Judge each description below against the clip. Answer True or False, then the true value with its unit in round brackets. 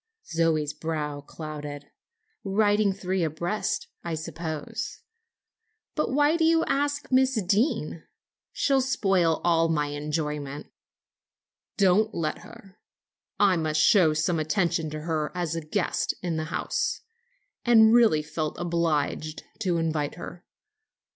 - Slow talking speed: True (120 wpm)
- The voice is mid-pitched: True (165 Hz)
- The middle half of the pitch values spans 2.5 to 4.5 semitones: False (4.9 semitones)